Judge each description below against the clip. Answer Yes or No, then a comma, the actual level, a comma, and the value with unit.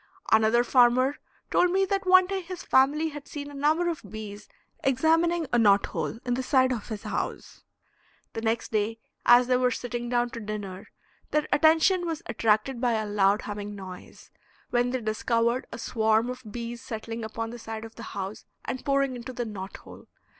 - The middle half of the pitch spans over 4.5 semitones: No, average, 4.1 semitones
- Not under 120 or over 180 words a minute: No, average, 190 wpm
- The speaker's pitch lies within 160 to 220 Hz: No, high, 240 Hz